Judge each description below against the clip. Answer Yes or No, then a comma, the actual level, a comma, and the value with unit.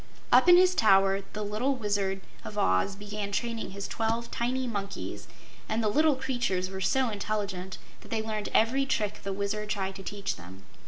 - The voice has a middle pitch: No, high, 210 Hz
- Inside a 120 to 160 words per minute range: No, average, 180 wpm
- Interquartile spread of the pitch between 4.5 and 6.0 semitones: No, average, 3.0 semitones